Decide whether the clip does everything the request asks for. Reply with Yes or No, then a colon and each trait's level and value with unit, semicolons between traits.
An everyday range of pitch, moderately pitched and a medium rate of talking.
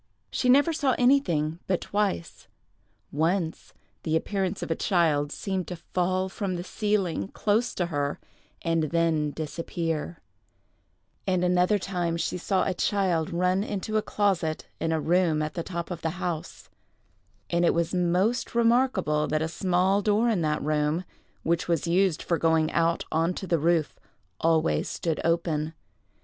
Yes: average, 3.0 semitones; medium, 175 Hz; average, 160 wpm